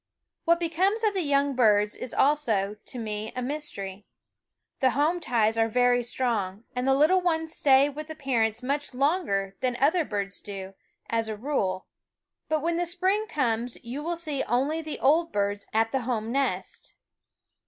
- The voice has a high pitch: Yes, very high, 260 Hz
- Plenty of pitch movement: Yes, wide, 5.8 semitones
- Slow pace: No, average, 175 wpm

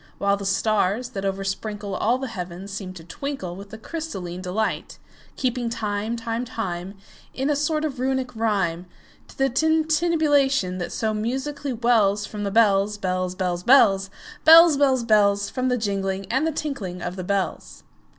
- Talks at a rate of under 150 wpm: Yes, average, 140 wpm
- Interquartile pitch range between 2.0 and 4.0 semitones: No, average, 5.2 semitones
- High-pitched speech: Yes, high, 215 Hz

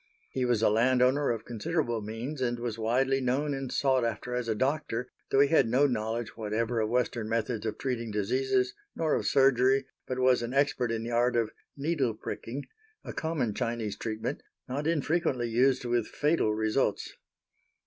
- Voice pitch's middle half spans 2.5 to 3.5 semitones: Yes, average, 2.9 semitones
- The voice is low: Yes, low, 125 Hz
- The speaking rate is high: No, average, 175 wpm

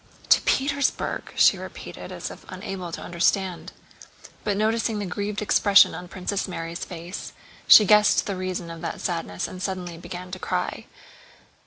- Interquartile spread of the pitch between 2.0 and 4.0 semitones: Yes, average, 2.8 semitones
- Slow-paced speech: No, average, 155 wpm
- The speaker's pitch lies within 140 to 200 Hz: Yes, medium, 185 Hz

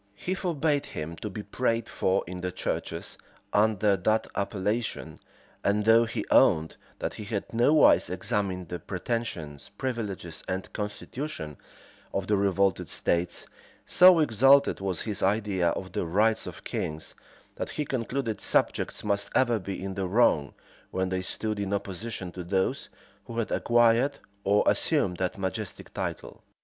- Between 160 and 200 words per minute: No, average, 150 wpm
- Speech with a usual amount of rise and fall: Yes, average, 3.8 semitones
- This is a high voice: No, low, 100 Hz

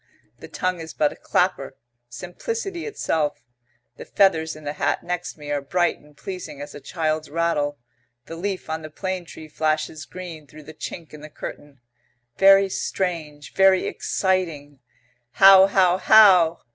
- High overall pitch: No, medium, 165 Hz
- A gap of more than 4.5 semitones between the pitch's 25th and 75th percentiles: No, average, 3.8 semitones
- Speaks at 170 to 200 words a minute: No, average, 160 wpm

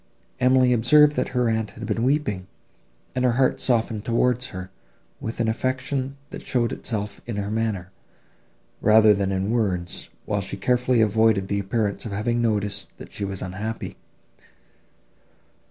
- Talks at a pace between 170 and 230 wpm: No, average, 155 wpm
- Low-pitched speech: Yes, low, 110 Hz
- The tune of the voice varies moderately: Yes, average, 3.5 semitones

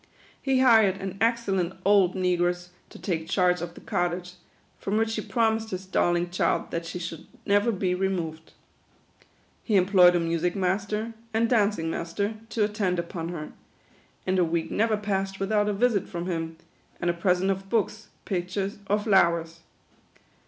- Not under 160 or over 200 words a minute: Yes, average, 165 wpm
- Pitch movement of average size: Yes, average, 3.0 semitones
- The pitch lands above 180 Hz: Yes, high, 190 Hz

